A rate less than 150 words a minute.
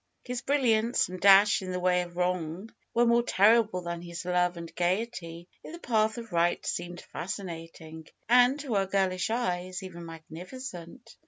No: average, 165 wpm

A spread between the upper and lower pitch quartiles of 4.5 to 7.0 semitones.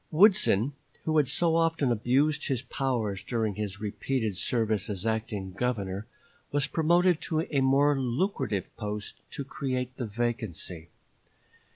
Yes: wide, 5.5 semitones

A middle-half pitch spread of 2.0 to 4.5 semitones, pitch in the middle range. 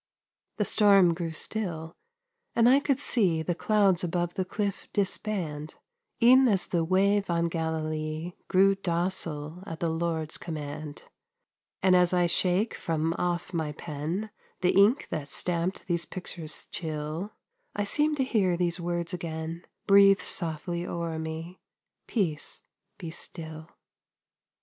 Yes: average, 3.3 semitones; medium, 175 Hz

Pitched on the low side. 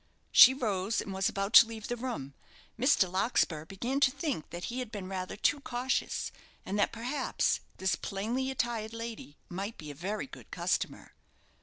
No: high, 220 Hz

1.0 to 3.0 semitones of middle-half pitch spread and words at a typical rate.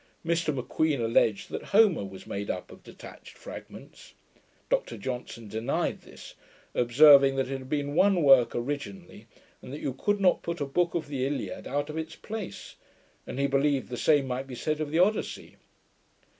No: average, 4.2 semitones; average, 180 wpm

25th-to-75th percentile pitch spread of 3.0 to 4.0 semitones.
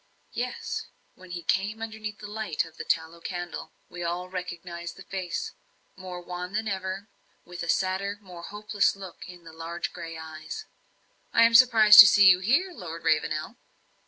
Yes: average, 3.3 semitones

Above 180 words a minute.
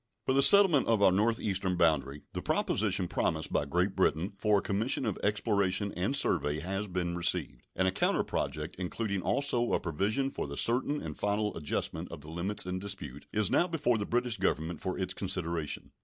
Yes: average, 190 wpm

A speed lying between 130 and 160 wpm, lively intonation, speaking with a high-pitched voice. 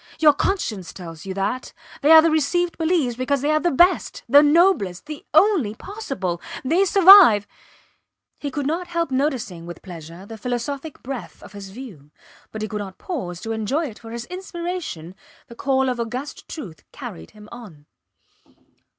No: average, 170 wpm; wide, 7.9 semitones; very high, 255 Hz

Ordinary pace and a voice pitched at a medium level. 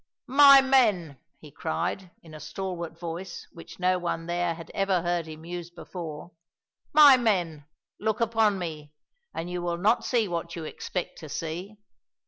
Yes: average, 160 wpm; medium, 175 Hz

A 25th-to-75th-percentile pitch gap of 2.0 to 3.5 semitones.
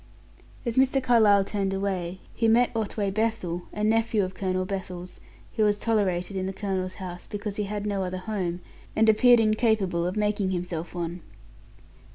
Yes: average, 2.9 semitones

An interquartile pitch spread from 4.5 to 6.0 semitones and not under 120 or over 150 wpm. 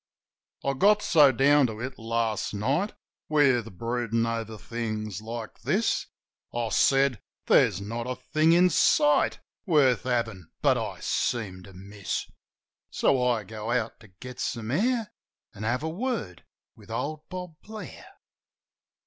Yes: average, 5.0 semitones; average, 140 wpm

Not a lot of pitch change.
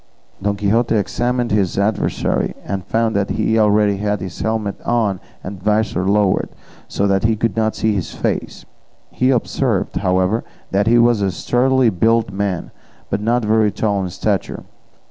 Yes: narrow, 2.3 semitones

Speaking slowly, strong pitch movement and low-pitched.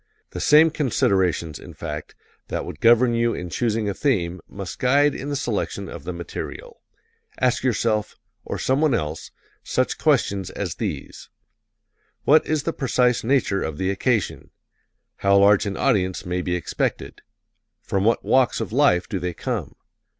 No: average, 155 wpm; wide, 6.0 semitones; low, 110 Hz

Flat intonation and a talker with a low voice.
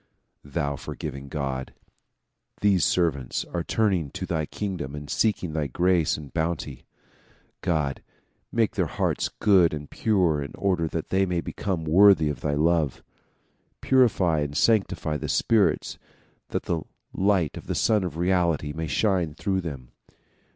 No: average, 4.4 semitones; very low, 85 Hz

